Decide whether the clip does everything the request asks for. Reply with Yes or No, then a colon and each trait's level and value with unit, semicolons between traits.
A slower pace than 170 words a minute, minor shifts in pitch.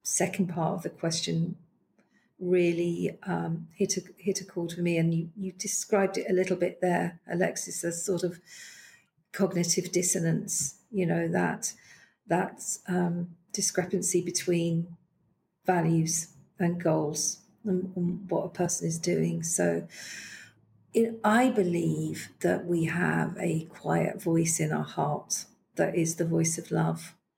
Yes: average, 140 wpm; narrow, 2.0 semitones